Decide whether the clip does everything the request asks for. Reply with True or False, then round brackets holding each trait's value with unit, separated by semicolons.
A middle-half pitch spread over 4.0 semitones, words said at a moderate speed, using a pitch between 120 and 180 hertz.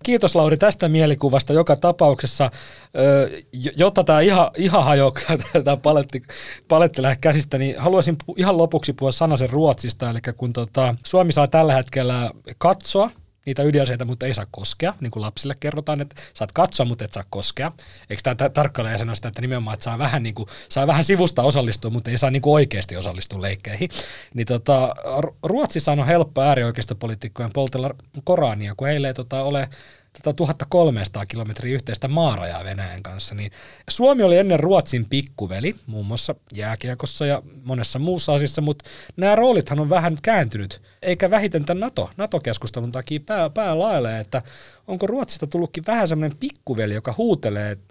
False (5.3 semitones; 160 wpm; 140 Hz)